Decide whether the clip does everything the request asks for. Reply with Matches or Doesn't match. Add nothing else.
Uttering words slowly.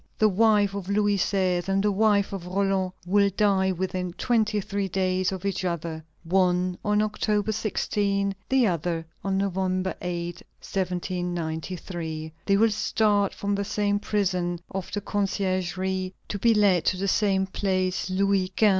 Doesn't match